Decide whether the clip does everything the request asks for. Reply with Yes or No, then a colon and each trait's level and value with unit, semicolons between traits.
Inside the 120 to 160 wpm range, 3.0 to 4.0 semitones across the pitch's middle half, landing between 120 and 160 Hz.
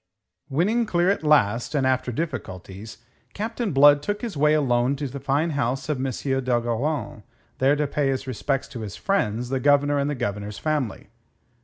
No: average, 175 wpm; average, 3.6 semitones; medium, 140 Hz